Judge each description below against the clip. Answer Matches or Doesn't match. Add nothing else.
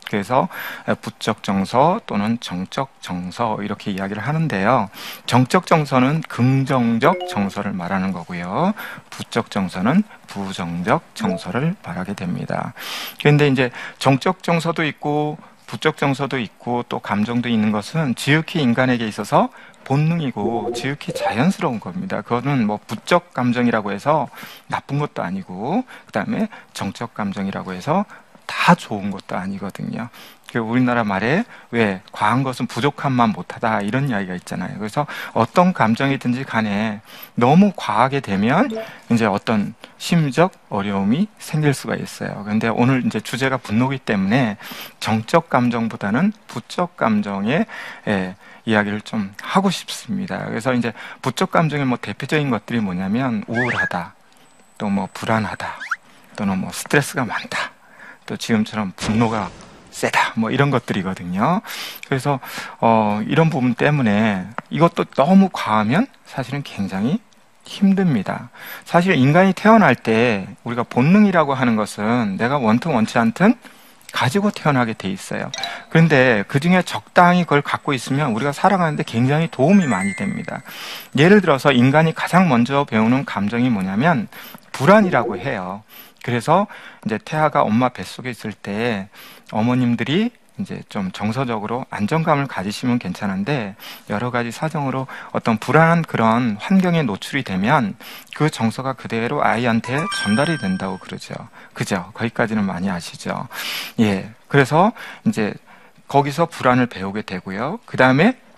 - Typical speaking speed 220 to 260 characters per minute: Doesn't match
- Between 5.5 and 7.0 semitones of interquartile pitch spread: Doesn't match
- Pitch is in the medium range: Doesn't match